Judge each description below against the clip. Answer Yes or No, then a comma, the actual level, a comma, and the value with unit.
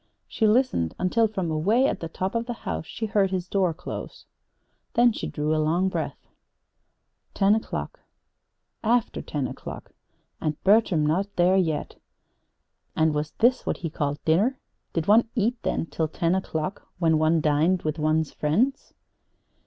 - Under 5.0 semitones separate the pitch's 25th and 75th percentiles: No, wide, 5.5 semitones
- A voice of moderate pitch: Yes, medium, 180 Hz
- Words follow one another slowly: No, average, 160 wpm